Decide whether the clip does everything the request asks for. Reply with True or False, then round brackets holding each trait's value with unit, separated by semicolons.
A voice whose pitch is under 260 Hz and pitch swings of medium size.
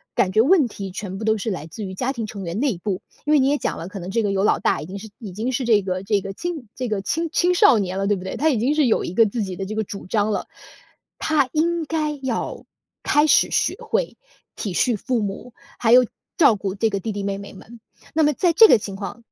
False (220 Hz; 5.8 semitones)